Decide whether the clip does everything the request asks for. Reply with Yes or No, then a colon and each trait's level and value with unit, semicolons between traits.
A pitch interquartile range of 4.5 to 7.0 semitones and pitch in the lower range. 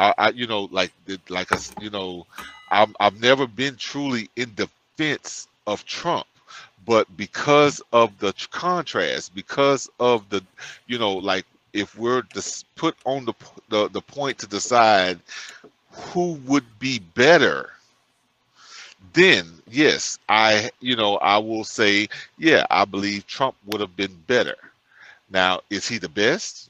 Yes: average, 5.1 semitones; low, 110 Hz